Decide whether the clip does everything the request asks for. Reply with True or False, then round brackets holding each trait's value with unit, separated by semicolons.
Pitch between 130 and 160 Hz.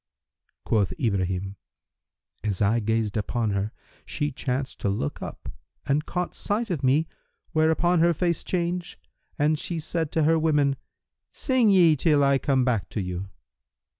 True (140 Hz)